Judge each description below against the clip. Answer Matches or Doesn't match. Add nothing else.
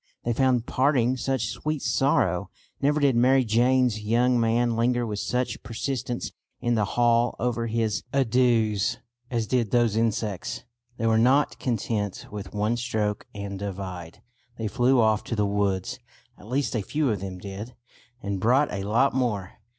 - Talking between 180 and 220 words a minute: Doesn't match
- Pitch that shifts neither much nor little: Matches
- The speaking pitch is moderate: Doesn't match